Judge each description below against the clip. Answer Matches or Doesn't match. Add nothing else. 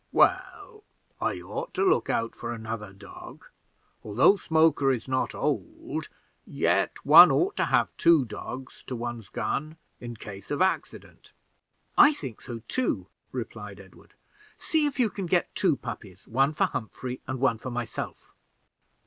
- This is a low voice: Matches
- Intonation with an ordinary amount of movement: Doesn't match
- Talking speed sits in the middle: Matches